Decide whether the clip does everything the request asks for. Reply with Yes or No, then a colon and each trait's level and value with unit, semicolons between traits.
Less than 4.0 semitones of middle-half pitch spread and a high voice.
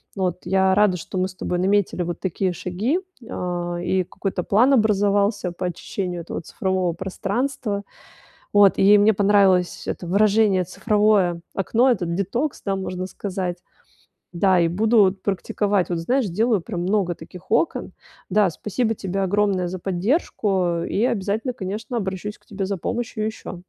Yes: narrow, 2.6 semitones; high, 195 Hz